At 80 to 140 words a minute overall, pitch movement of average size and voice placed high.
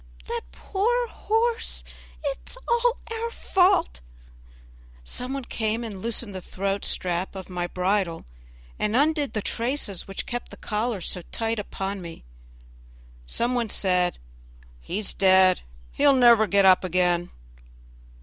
No: slow, 135 wpm; wide, 6.3 semitones; high, 210 Hz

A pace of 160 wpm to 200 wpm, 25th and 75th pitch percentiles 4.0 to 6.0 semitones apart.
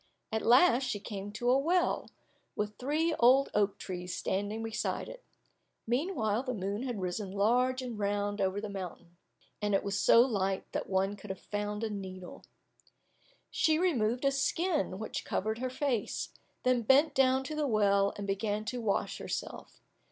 Yes: average, 170 wpm; average, 4.4 semitones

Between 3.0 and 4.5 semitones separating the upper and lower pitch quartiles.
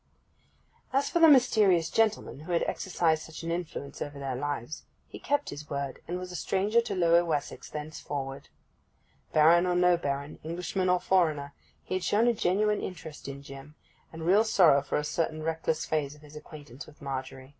Yes: average, 4.1 semitones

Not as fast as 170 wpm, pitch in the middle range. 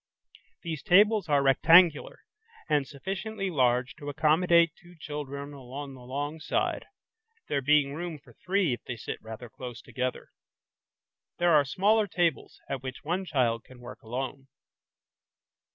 Yes: average, 140 wpm; medium, 145 Hz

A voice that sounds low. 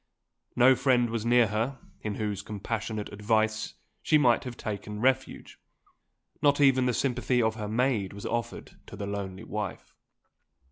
Yes: low, 110 Hz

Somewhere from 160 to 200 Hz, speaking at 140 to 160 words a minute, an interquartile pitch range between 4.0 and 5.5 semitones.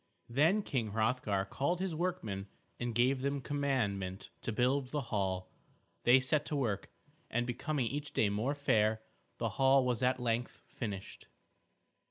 No: low, 125 Hz; average, 150 wpm; average, 4.4 semitones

